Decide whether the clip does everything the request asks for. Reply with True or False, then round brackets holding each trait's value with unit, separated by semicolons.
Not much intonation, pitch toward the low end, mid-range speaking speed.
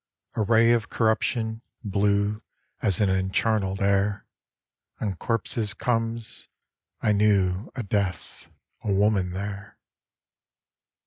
False (2.3 semitones; 105 Hz; 105 wpm)